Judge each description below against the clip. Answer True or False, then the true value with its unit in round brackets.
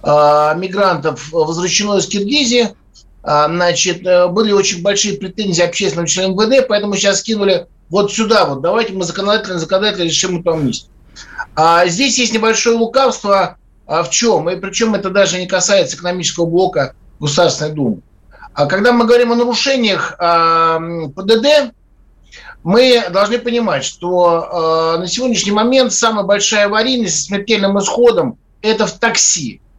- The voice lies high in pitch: True (195 Hz)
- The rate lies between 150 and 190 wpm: False (135 wpm)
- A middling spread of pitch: True (4.6 semitones)